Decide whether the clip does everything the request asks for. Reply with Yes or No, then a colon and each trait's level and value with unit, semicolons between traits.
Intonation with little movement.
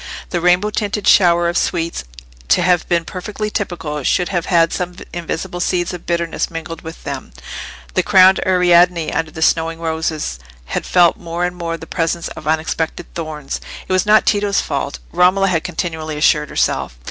Yes: narrow, 1.8 semitones